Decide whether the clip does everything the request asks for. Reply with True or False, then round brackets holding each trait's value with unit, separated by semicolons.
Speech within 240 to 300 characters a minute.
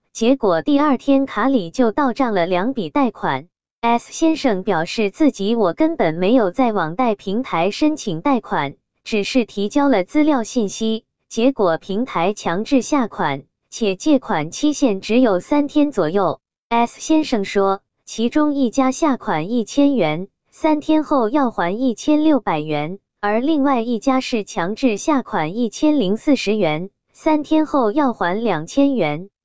False (225 characters per minute)